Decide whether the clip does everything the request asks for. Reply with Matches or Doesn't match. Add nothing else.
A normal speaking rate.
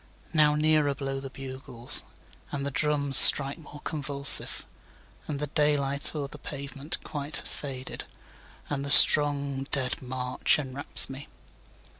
Doesn't match